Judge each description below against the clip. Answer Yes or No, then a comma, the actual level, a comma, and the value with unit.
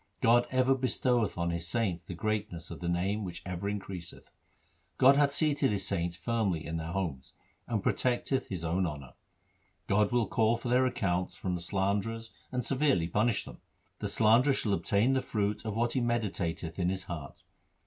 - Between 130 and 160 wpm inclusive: No, average, 185 wpm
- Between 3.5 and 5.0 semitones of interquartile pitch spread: No, wide, 5.4 semitones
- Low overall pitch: Yes, low, 100 Hz